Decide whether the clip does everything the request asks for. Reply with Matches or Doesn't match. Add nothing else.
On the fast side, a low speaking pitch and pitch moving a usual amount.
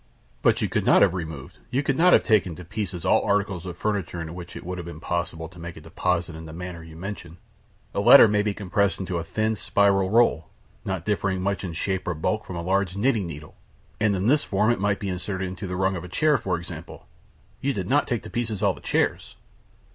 Matches